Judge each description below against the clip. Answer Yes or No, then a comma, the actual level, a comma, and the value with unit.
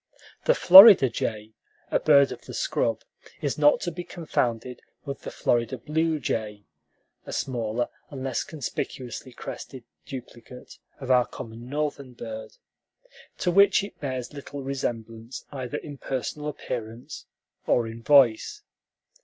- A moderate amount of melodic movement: Yes, average, 4.0 semitones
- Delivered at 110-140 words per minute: Yes, slow, 135 wpm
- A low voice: Yes, low, 130 Hz